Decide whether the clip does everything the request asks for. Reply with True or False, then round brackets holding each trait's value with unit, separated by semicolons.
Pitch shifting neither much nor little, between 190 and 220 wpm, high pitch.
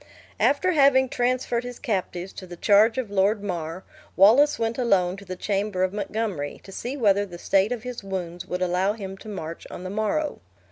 True (4.4 semitones; 195 wpm; 205 Hz)